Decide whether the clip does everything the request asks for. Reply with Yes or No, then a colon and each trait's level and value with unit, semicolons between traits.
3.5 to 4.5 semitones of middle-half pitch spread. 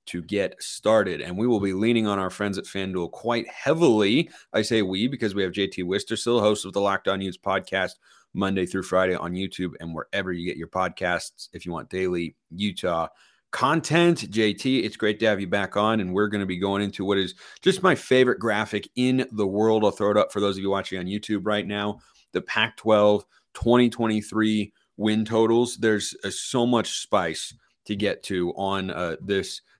No: narrow, 2.4 semitones